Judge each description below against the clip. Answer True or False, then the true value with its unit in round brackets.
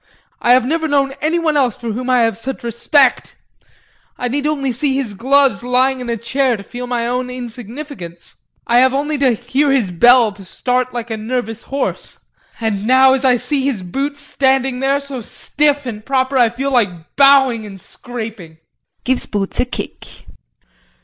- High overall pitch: True (250 Hz)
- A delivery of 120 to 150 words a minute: False (185 wpm)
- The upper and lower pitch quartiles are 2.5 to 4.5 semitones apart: True (2.9 semitones)